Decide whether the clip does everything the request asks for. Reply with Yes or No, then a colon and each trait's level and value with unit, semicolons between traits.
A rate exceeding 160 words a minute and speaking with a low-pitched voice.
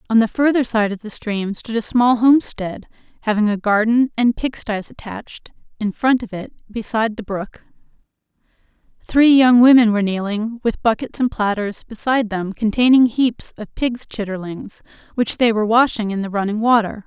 No: average, 170 wpm; high, 225 Hz